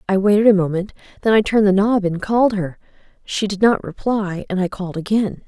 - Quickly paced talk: Yes, fast, 220 wpm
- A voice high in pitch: Yes, high, 200 Hz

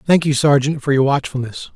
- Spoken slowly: No, fast, 205 wpm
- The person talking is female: No, male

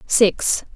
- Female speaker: Yes, female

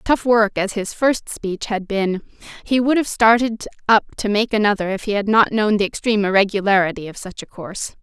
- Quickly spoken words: Yes, fast, 210 wpm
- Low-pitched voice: No, high, 210 Hz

